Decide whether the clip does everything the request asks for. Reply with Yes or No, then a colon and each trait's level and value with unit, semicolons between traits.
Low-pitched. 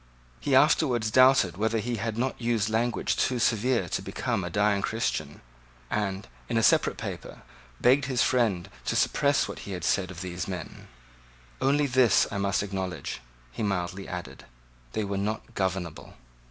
Yes: low, 105 Hz